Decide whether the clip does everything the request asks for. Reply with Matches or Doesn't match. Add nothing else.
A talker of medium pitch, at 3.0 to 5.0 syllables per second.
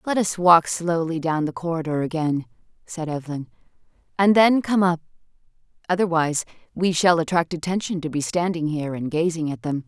Doesn't match